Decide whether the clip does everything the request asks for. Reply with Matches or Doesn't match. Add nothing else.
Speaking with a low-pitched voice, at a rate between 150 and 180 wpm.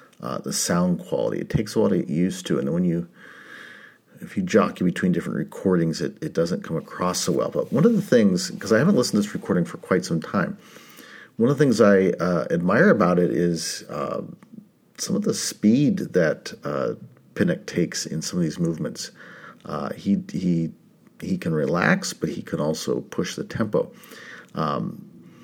Doesn't match